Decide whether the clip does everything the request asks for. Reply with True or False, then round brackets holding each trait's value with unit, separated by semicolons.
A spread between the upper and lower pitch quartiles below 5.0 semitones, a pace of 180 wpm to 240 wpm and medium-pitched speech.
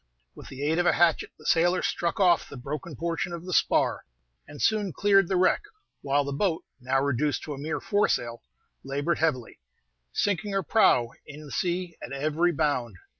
True (4.0 semitones; 185 wpm; 160 Hz)